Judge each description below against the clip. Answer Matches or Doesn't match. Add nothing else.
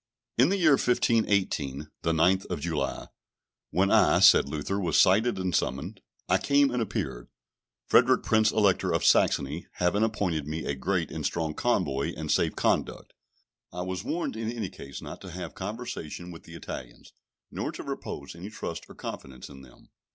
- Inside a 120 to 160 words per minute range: Doesn't match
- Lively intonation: Matches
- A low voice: Matches